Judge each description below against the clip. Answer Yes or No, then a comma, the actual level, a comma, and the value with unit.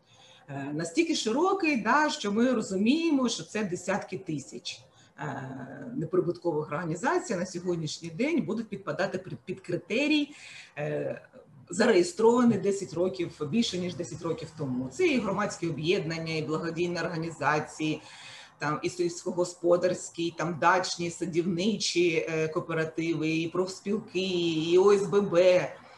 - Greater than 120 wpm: No, average, 110 wpm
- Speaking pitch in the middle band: Yes, medium, 175 Hz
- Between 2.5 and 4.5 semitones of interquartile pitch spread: Yes, average, 3.9 semitones